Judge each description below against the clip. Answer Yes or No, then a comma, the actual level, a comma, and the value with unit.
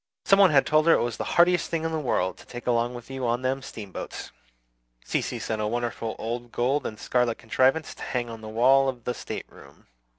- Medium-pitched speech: No, low, 125 Hz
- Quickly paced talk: Yes, fast, 225 wpm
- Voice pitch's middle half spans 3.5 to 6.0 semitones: No, average, 2.8 semitones